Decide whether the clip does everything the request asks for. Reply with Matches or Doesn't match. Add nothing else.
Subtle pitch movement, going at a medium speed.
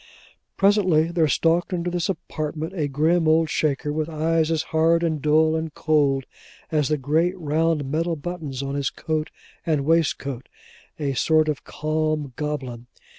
Matches